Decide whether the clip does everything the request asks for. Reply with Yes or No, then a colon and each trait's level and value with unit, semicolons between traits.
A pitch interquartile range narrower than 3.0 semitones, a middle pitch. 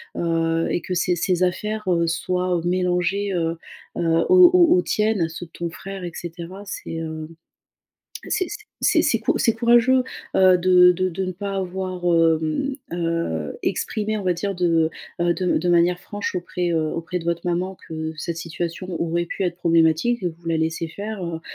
Yes: narrow, 2.5 semitones; medium, 175 Hz